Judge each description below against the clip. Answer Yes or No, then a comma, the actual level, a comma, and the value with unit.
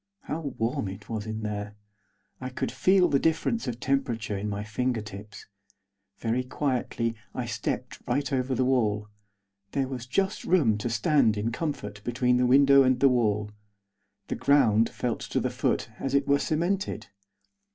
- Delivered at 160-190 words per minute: Yes, average, 165 wpm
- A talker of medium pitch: No, low, 125 Hz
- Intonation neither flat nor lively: Yes, average, 4.2 semitones